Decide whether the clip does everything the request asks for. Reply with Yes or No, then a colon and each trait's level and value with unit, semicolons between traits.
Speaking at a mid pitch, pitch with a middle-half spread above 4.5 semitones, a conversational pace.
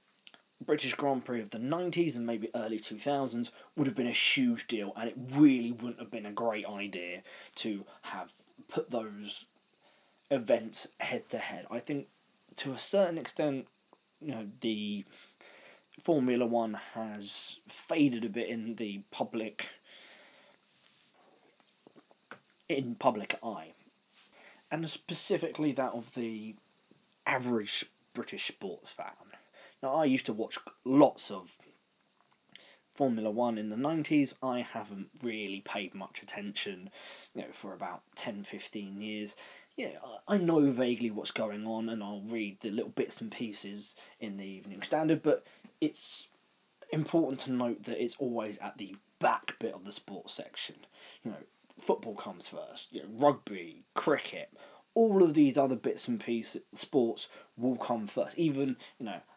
No: low, 120 Hz; average, 5.1 semitones; average, 150 wpm